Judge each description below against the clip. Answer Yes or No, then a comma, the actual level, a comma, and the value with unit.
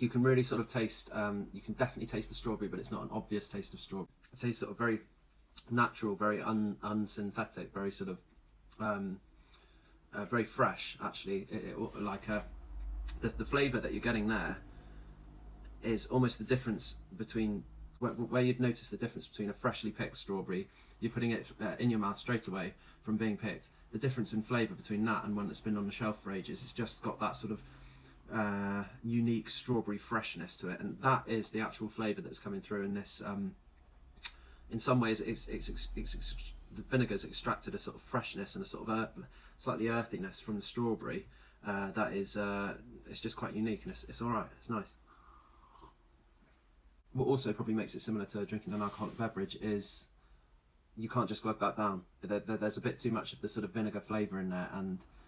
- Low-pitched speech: Yes, low, 105 Hz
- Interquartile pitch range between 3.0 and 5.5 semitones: No, narrow, 2.4 semitones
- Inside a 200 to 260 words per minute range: Yes, fast, 205 wpm